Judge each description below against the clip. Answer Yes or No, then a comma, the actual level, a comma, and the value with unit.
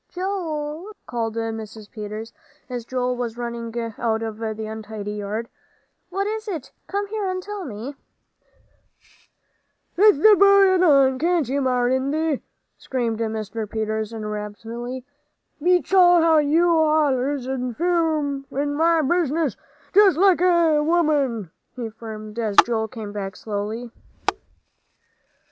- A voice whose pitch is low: No, very high, 260 Hz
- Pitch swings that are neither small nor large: No, wide, 7.1 semitones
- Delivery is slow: Yes, slow, 120 wpm